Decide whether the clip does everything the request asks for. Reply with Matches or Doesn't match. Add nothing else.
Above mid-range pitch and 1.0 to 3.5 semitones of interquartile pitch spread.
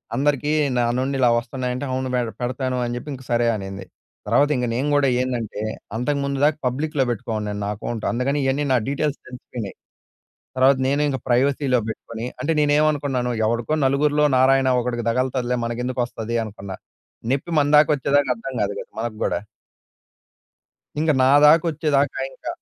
Doesn't match